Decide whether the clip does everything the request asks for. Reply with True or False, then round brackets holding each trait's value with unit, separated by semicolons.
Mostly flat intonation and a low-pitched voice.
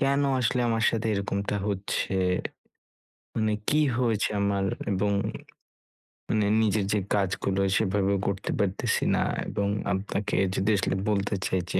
True (1.8 semitones; 100 Hz)